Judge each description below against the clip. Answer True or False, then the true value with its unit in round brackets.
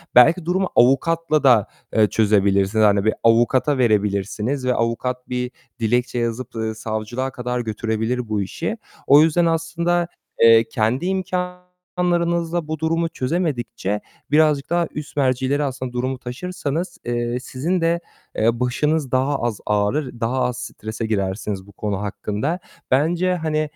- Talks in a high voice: False (125 Hz)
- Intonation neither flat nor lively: False (6.2 semitones)